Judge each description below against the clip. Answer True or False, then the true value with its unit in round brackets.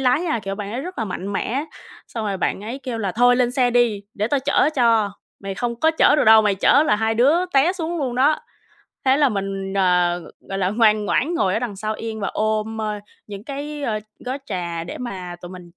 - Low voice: False (220 Hz)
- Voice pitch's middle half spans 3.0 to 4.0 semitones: False (4.8 semitones)